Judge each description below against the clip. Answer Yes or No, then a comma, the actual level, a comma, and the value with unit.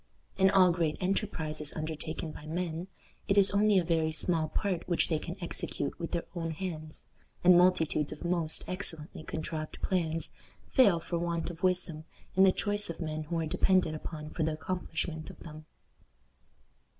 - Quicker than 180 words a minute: No, average, 175 wpm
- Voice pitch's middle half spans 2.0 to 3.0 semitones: Yes, average, 2.7 semitones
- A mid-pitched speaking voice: Yes, medium, 170 Hz